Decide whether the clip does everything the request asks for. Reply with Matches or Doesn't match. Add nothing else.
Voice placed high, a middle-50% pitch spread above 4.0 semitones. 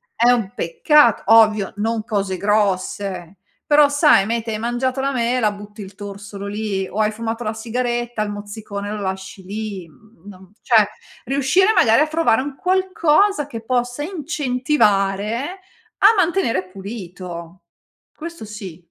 Matches